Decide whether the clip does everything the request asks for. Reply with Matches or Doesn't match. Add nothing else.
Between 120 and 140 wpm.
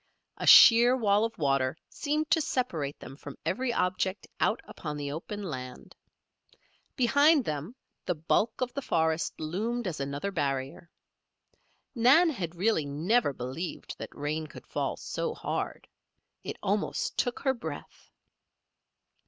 Matches